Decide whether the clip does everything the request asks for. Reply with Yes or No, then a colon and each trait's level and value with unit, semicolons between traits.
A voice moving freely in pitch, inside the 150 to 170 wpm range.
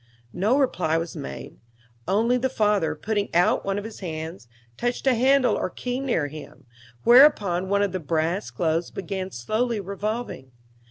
Yes: wide, 6.1 semitones; average, 160 wpm